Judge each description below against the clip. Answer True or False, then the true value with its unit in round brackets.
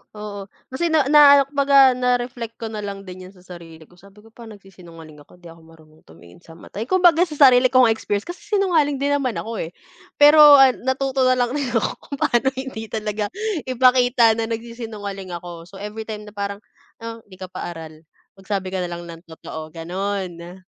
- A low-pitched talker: False (215 Hz)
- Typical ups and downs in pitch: False (6.1 semitones)